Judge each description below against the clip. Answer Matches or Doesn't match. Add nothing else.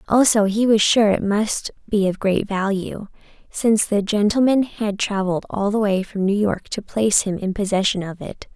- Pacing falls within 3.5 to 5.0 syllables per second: Matches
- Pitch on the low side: Doesn't match